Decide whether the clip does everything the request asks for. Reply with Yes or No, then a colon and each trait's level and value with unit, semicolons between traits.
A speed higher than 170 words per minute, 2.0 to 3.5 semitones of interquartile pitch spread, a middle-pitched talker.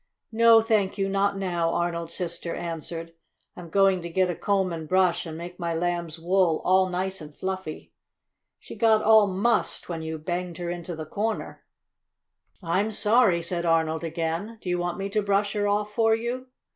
Yes: average, 185 wpm; average, 3.2 semitones; medium, 180 Hz